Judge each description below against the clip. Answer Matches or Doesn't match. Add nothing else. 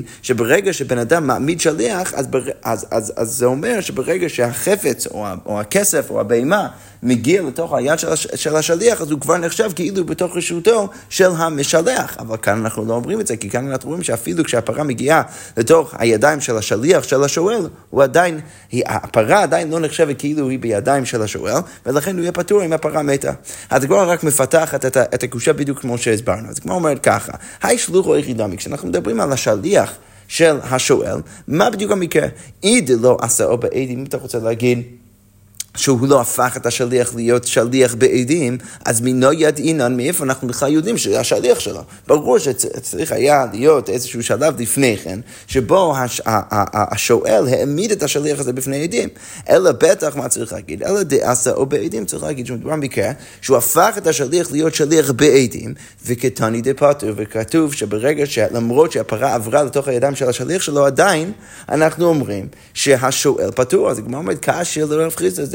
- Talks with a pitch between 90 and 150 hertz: Matches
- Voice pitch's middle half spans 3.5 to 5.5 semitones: Matches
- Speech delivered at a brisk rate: Matches